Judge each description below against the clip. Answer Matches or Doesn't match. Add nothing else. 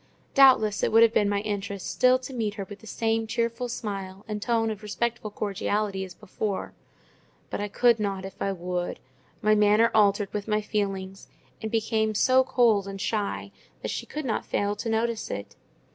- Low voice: Doesn't match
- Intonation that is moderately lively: Doesn't match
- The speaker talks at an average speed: Matches